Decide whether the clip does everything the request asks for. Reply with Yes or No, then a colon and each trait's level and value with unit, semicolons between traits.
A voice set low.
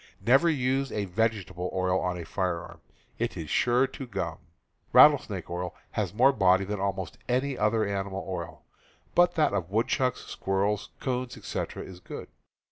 Yes: low, 100 Hz